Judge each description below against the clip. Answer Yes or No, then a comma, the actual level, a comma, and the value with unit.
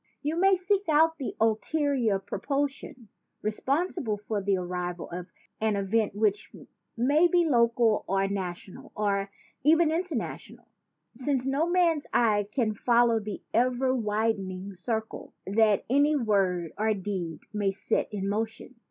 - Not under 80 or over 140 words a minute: Yes, slow, 135 wpm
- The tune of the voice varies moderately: No, wide, 5.8 semitones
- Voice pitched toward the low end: No, high, 225 Hz